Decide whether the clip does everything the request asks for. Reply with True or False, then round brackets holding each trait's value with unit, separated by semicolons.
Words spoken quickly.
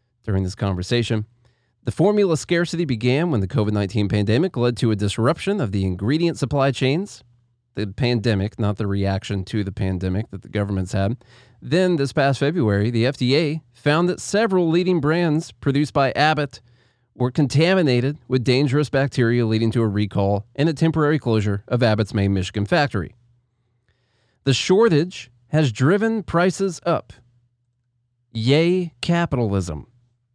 False (140 wpm)